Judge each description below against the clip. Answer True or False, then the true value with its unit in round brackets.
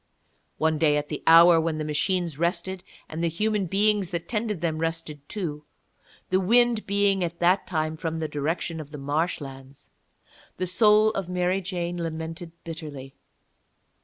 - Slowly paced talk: False (160 wpm)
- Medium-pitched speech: True (170 Hz)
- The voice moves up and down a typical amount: True (3.1 semitones)